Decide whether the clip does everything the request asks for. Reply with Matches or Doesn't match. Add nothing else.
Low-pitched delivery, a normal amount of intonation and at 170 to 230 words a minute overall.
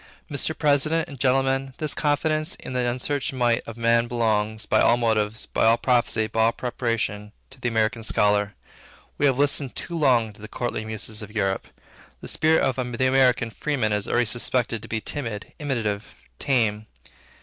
Matches